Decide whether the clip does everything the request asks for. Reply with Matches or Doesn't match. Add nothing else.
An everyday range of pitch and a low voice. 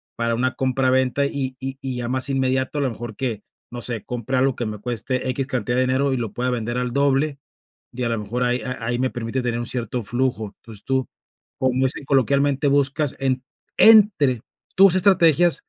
Doesn't match